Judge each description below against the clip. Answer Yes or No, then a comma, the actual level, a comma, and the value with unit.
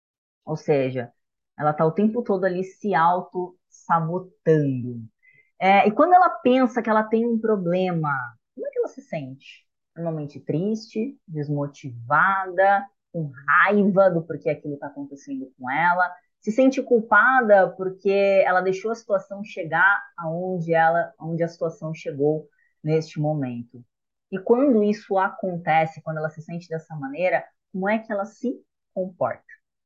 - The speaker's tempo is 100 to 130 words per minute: No, average, 140 wpm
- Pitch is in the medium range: Yes, medium, 180 Hz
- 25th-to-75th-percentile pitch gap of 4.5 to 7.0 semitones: Yes, average, 4.9 semitones